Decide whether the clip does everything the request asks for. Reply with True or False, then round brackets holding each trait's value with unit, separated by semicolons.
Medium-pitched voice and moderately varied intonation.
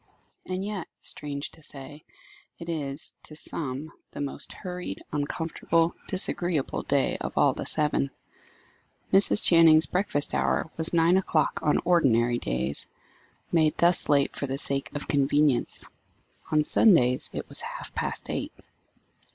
True (150 Hz; 3.3 semitones)